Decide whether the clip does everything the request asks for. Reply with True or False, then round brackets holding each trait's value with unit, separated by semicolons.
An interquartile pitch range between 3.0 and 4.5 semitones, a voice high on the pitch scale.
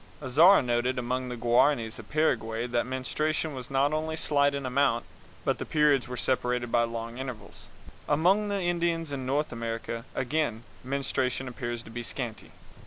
False (3.8 semitones; 130 Hz)